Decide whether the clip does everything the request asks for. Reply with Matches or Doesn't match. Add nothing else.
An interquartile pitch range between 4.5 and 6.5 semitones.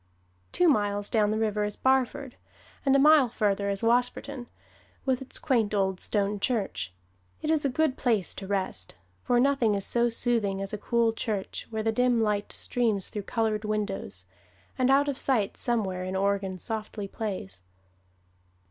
Doesn't match